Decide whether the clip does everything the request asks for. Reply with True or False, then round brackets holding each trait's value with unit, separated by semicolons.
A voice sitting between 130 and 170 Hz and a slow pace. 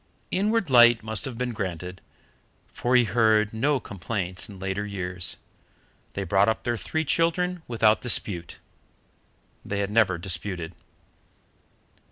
False (110 Hz; 130 wpm)